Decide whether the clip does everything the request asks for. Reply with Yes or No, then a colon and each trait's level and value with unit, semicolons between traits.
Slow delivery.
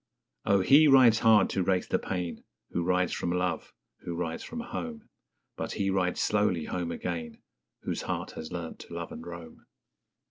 No: average, 175 wpm